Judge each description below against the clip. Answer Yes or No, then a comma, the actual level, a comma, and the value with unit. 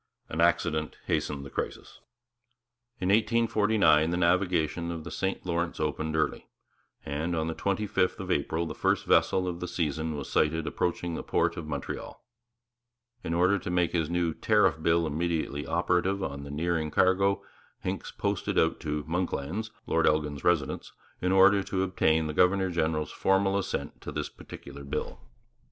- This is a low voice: Yes, very low, 85 Hz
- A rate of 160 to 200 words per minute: Yes, average, 165 wpm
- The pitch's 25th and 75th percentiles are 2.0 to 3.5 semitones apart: Yes, average, 2.9 semitones